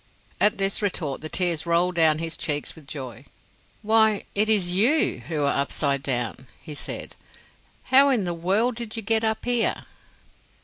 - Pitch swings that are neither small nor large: No, wide, 6.4 semitones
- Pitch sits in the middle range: Yes, medium, 180 Hz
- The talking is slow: No, average, 175 wpm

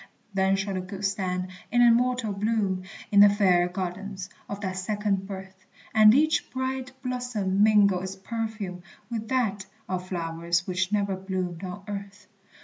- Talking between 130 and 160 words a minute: Yes, average, 150 wpm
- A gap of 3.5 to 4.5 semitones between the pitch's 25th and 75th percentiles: No, narrow, 2.5 semitones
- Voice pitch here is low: No, high, 195 Hz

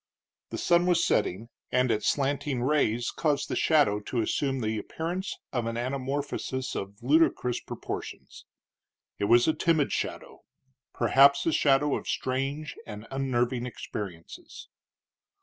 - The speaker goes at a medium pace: No, slow, 130 wpm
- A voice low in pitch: Yes, low, 130 Hz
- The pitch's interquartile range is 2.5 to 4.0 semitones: Yes, average, 3.7 semitones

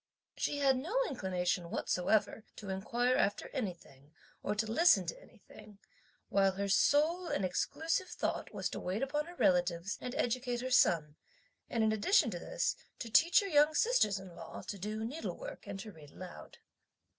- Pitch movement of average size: No, wide, 7.4 semitones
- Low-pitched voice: No, high, 220 Hz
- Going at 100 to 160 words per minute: No, average, 170 wpm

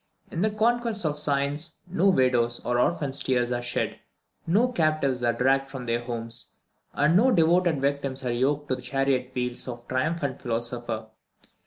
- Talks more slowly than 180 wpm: Yes, average, 170 wpm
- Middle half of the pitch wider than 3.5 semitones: Yes, average, 4.5 semitones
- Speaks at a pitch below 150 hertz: Yes, low, 135 Hz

